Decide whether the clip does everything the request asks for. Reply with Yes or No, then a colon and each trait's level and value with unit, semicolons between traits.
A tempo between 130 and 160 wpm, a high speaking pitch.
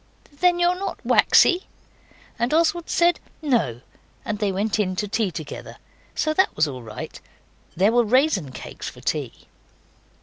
Yes: average, 155 wpm; high, 230 Hz